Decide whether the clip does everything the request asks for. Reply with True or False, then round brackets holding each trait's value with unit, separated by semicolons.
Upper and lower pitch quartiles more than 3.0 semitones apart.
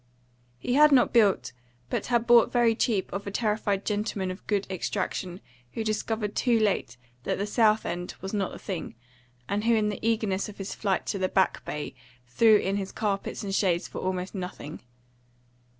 False (2.7 semitones)